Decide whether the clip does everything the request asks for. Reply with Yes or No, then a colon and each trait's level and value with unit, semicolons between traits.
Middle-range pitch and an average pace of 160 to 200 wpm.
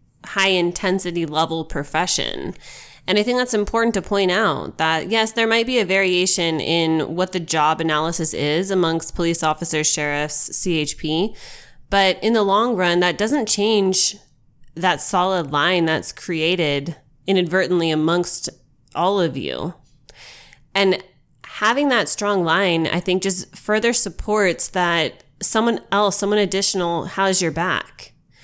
No: medium, 180 Hz; average, 140 wpm